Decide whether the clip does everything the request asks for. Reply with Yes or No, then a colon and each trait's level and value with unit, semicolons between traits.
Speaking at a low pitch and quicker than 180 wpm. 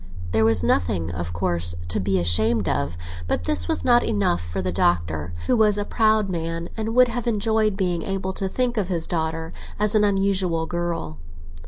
No: medium, 165 Hz; average, 190 wpm